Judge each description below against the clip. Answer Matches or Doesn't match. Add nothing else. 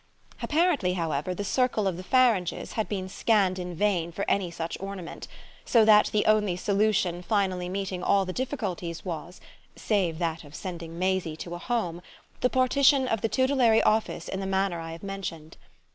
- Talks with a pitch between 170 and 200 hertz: Matches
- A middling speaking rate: Matches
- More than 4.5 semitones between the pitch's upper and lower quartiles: Doesn't match